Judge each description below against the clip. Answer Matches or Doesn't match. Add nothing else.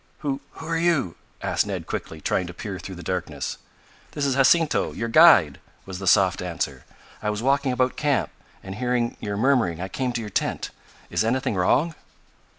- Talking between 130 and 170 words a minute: Doesn't match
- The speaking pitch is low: Matches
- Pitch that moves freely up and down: Matches